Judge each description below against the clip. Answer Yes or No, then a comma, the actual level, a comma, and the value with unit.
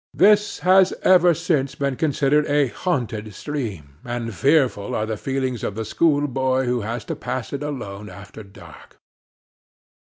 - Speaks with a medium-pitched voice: No, low, 130 Hz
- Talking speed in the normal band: Yes, average, 150 wpm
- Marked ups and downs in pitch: No, average, 5.0 semitones